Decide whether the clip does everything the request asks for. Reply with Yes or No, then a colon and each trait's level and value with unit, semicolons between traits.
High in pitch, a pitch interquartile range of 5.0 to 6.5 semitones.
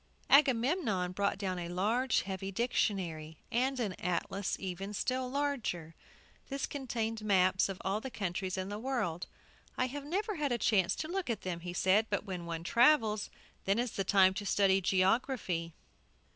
Yes: high, 205 Hz; wide, 5.4 semitones